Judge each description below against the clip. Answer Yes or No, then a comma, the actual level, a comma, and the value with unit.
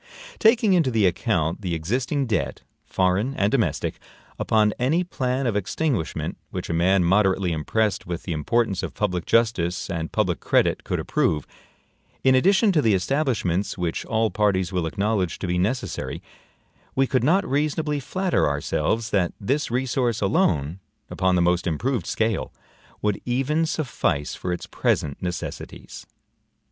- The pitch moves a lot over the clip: Yes, wide, 6.7 semitones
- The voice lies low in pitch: Yes, low, 105 Hz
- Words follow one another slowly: No, average, 150 wpm